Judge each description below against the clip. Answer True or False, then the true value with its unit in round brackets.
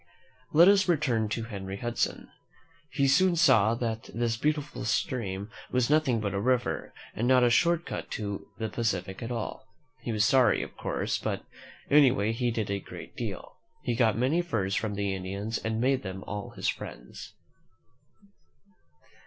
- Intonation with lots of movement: False (4.2 semitones)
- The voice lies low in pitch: True (115 Hz)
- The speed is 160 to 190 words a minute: True (165 wpm)